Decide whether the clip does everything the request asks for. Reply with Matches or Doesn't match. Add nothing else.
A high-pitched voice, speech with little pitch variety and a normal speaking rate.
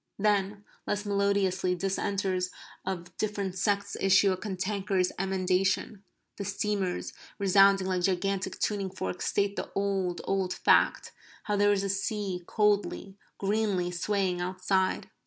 Doesn't match